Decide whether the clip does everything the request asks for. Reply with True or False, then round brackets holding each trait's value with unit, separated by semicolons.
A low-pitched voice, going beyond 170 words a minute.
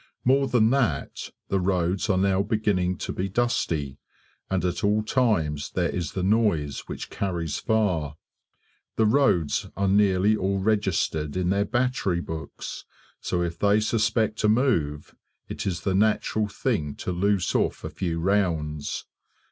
False (95 Hz; 150 wpm)